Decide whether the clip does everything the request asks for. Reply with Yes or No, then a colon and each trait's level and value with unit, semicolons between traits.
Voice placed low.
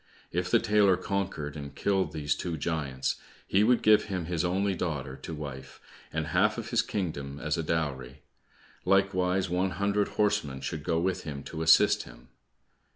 Yes: very low, 85 Hz